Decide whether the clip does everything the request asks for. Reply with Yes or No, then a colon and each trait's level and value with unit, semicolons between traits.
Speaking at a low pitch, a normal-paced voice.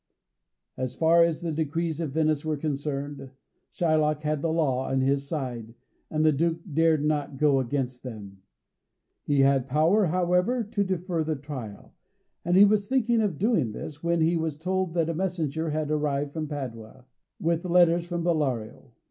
No: medium, 155 Hz; average, 170 wpm